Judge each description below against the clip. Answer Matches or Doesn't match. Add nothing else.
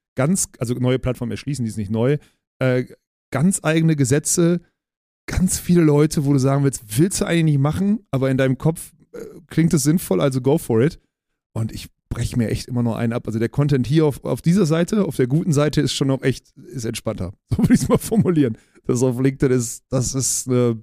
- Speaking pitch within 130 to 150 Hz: Matches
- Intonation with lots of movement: Doesn't match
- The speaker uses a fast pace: Matches